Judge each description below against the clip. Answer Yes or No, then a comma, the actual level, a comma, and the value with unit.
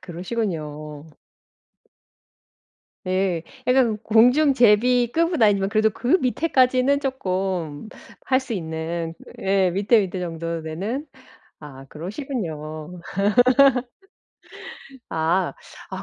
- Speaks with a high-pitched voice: Yes, high, 195 Hz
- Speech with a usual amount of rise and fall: No, wide, 7.1 semitones